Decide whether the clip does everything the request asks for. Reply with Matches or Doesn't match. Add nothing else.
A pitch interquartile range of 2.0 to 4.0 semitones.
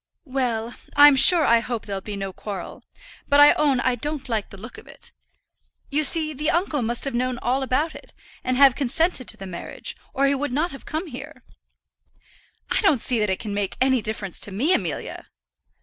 Doesn't match